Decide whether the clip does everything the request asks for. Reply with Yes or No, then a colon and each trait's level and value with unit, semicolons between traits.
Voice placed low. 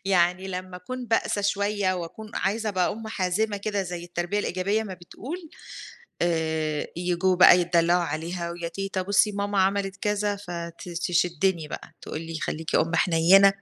No: medium, 185 Hz